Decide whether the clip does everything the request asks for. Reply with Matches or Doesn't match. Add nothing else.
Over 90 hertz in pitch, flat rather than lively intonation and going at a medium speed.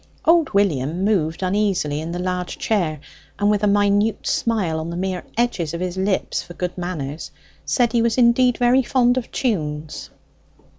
Doesn't match